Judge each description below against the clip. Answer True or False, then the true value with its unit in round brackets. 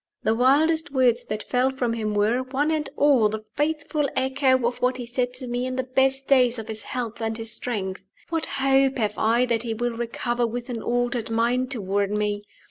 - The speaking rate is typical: False (210 wpm)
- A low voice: False (245 Hz)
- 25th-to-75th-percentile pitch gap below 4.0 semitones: True (2.8 semitones)